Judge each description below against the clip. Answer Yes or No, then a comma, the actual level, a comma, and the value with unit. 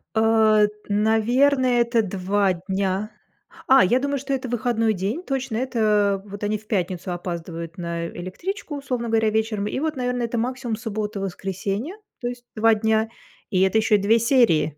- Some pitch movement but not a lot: Yes, average, 3.7 semitones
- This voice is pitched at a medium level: No, high, 220 Hz